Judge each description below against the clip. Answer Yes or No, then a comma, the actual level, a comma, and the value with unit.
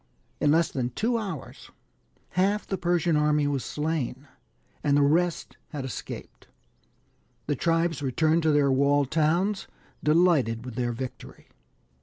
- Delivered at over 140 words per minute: No, slow, 135 wpm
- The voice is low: No, medium, 150 Hz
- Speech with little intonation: No, average, 3.5 semitones